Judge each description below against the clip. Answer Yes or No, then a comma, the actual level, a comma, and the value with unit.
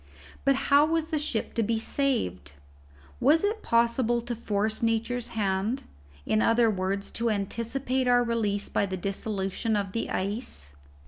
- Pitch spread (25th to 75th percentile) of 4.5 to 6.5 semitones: No, average, 3.6 semitones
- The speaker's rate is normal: Yes, average, 150 wpm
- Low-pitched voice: No, high, 230 Hz